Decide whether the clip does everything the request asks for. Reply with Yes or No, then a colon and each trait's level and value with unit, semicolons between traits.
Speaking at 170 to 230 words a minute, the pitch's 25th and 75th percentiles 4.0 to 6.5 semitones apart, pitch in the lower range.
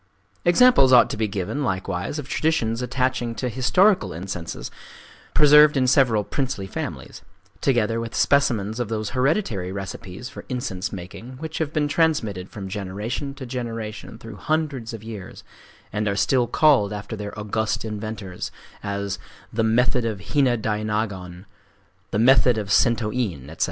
No: average, 145 wpm; average, 4.4 semitones; low, 115 Hz